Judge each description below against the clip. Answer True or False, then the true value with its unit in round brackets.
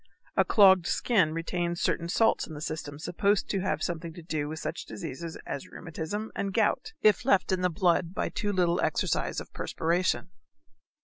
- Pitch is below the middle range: False (175 Hz)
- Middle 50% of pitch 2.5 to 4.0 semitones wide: True (3.3 semitones)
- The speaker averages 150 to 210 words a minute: True (180 wpm)